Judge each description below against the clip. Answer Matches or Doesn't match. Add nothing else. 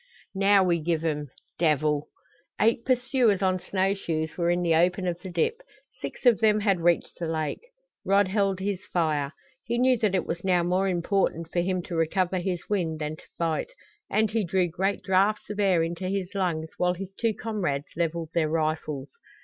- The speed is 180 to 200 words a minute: Matches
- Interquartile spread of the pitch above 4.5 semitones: Doesn't match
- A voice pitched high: Doesn't match